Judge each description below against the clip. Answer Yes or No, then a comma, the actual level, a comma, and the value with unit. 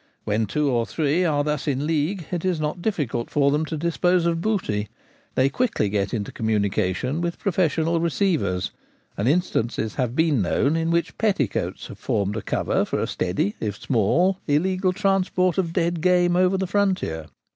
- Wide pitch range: Yes, wide, 7.4 semitones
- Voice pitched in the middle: Yes, medium, 155 Hz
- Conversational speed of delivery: Yes, average, 175 wpm